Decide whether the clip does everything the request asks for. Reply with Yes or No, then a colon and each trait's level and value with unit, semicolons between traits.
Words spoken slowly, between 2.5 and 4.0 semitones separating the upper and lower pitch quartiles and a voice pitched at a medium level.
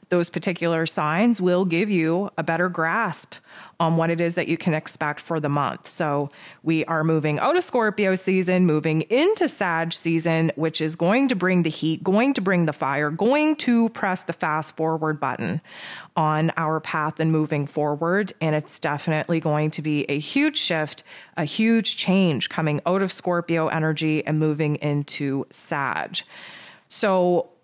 No: average, 170 wpm; average, 3.1 semitones; medium, 165 Hz